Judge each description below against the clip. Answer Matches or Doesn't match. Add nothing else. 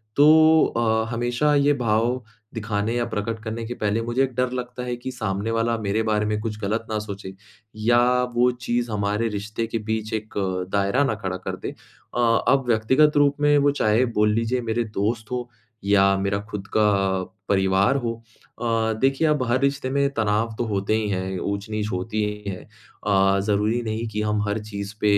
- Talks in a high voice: Doesn't match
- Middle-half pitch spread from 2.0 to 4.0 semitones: Matches